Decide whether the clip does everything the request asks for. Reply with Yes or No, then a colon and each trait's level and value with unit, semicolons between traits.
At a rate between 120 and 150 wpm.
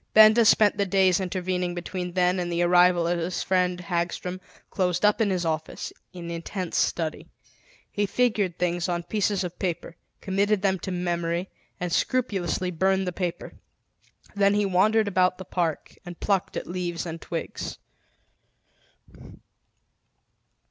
Yes: average, 145 wpm